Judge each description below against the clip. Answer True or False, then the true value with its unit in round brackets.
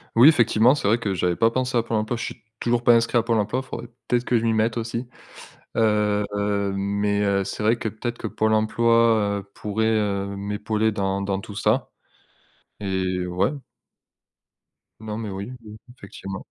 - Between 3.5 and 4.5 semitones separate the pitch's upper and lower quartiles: False (2.5 semitones)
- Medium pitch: False (110 Hz)